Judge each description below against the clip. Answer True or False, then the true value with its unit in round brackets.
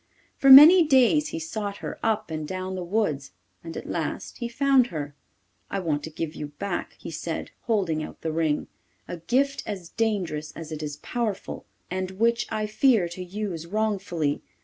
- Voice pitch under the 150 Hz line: False (190 Hz)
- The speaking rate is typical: True (180 wpm)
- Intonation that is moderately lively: False (5.8 semitones)